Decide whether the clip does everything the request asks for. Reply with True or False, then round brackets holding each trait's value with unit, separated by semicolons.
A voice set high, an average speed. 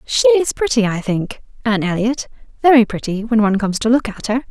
False (230 Hz; 215 wpm)